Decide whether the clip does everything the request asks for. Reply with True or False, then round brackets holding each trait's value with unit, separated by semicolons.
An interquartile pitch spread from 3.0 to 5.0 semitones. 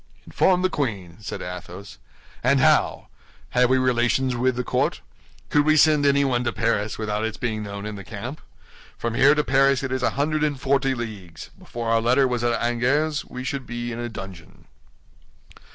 True (3.7 semitones)